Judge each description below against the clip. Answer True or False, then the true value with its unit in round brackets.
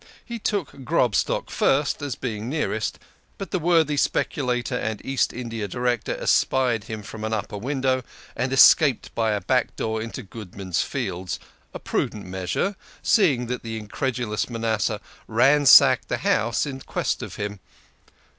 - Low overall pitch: True (120 Hz)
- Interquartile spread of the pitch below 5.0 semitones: True (3.9 semitones)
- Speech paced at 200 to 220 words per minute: False (145 wpm)